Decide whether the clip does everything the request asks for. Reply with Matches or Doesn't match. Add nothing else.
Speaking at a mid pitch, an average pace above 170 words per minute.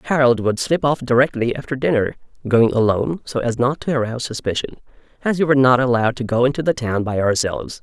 Doesn't match